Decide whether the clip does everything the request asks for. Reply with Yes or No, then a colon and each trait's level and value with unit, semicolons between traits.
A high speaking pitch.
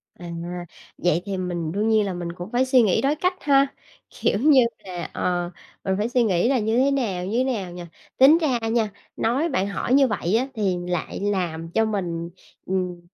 Yes: high, 210 Hz